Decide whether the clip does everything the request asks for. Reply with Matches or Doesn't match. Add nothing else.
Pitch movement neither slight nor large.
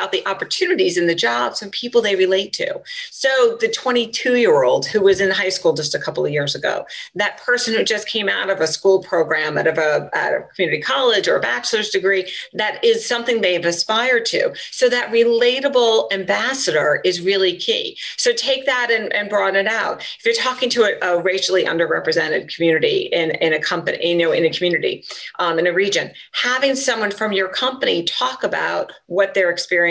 Doesn't match